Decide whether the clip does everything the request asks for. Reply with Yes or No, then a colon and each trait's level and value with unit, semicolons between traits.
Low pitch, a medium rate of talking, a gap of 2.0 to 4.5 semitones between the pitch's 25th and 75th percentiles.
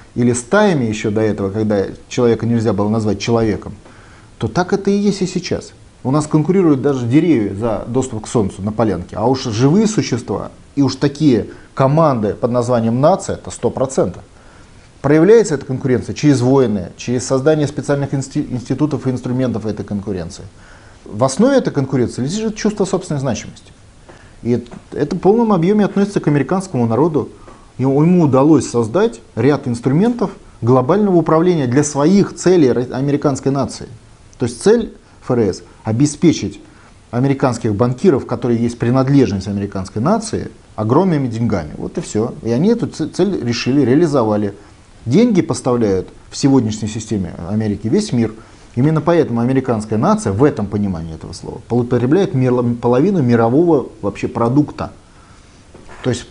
No: low, 125 Hz; average, 140 wpm; wide, 5.4 semitones